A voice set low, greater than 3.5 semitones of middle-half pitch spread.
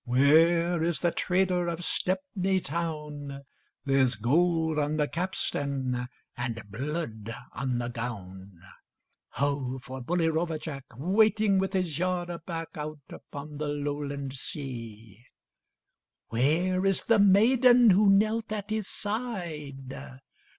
No: medium, 155 Hz; wide, 5.4 semitones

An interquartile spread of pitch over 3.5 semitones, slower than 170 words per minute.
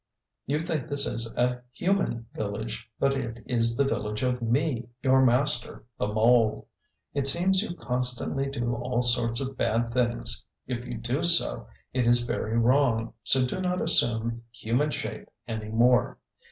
No: average, 2.8 semitones; average, 160 wpm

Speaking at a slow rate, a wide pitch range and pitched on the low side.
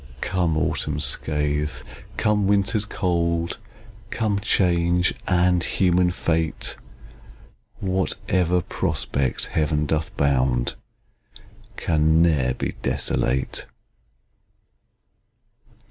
No: slow, 75 wpm; average, 3.4 semitones; very low, 85 Hz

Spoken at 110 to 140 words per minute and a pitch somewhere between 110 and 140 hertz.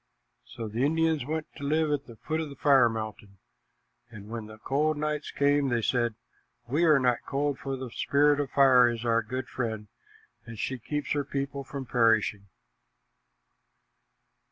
No: average, 170 wpm; low, 135 Hz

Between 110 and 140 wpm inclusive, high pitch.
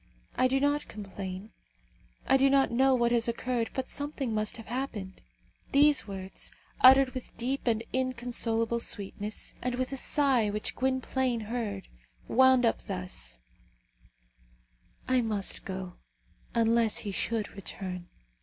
Yes: slow, 135 wpm; high, 235 Hz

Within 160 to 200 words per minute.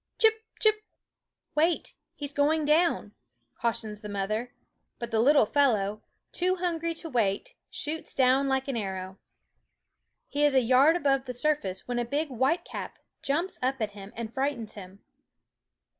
No: average, 150 wpm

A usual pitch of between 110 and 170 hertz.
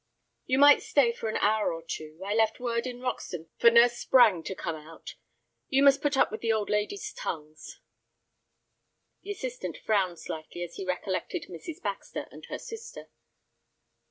No: high, 220 Hz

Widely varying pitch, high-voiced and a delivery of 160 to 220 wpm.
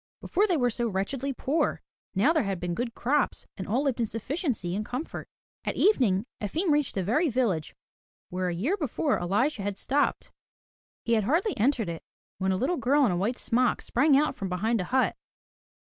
Yes: wide, 6.7 semitones; high, 240 Hz; average, 195 wpm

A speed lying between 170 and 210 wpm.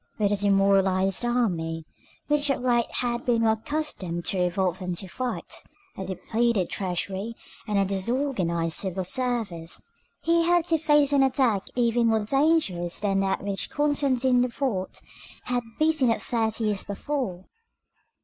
No: average, 145 wpm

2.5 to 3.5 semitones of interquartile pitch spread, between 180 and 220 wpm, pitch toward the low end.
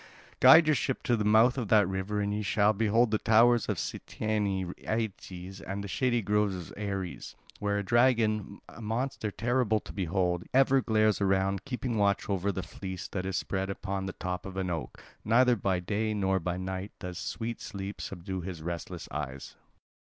Yes: average, 2.8 semitones; average, 185 wpm; low, 100 Hz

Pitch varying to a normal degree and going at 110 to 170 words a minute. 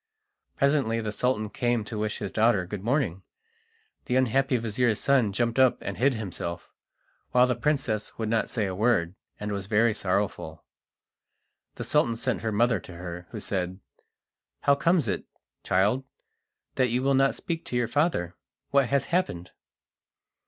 Yes: average, 4.2 semitones; average, 160 wpm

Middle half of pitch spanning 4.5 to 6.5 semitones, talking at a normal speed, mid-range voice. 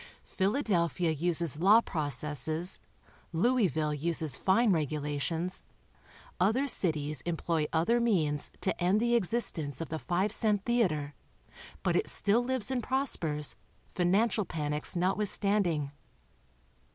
No: wide, 5.5 semitones; slow, 115 wpm; medium, 175 Hz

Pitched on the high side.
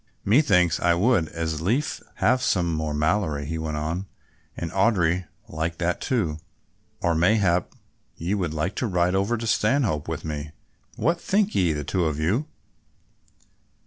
No: very low, 85 Hz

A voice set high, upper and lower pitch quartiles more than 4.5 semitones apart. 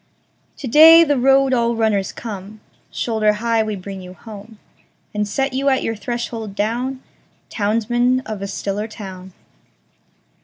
No: high, 225 Hz; average, 3.4 semitones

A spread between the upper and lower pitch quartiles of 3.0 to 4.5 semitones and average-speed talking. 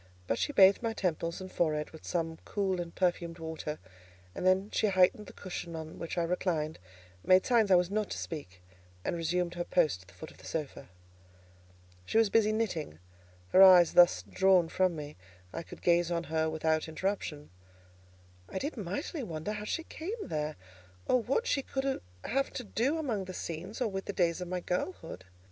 Yes: average, 4.2 semitones; average, 195 wpm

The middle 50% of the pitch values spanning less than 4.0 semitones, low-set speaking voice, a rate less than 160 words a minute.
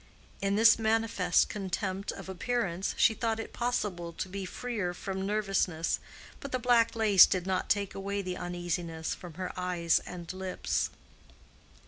No: average, 3.6 semitones; high, 190 Hz; average, 150 wpm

